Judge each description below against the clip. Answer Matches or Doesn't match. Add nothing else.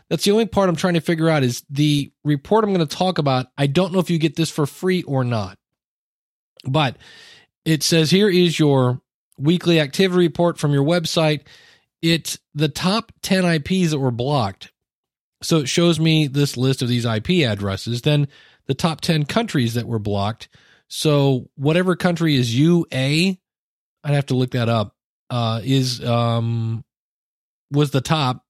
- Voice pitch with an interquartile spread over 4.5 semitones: Matches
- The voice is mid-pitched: Matches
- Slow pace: Doesn't match